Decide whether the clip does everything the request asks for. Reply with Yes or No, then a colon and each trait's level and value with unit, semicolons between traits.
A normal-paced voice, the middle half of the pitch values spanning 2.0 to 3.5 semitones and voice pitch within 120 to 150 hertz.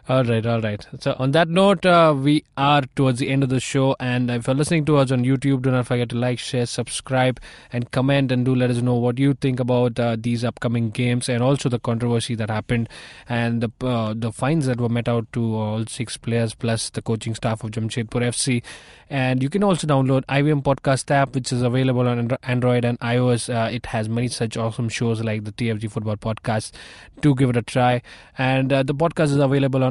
No: fast, 225 wpm; narrow, 2.5 semitones; low, 125 Hz